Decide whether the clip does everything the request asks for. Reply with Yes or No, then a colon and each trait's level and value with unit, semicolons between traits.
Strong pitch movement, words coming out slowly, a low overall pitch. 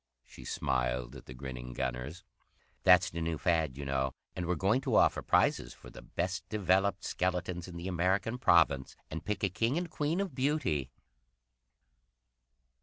No: wide, 6.2 semitones; average, 165 wpm; very low, 90 Hz